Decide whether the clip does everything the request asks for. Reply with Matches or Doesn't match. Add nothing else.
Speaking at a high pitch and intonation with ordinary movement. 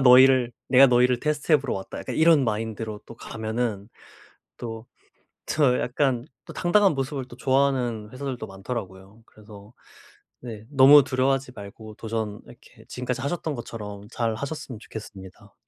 Doesn't match